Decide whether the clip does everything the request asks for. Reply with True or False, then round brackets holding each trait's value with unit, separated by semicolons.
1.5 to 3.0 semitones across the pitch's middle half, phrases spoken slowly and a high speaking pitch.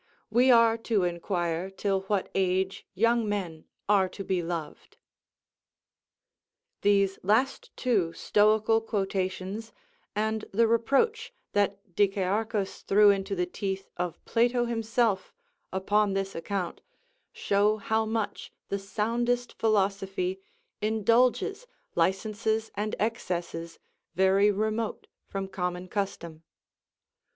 True (2.6 semitones; 105 wpm; 205 Hz)